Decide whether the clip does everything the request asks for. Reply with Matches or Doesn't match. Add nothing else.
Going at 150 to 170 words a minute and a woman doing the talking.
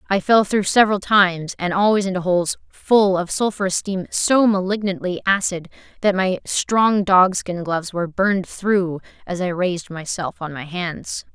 Matches